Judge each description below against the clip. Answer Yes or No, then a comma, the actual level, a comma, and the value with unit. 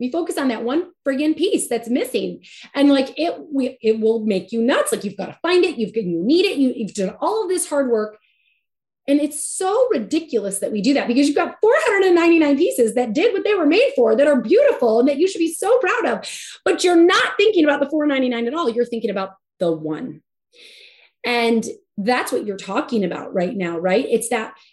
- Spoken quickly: Yes, fast, 225 wpm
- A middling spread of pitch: No, wide, 7.5 semitones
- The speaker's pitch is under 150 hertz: No, very high, 275 Hz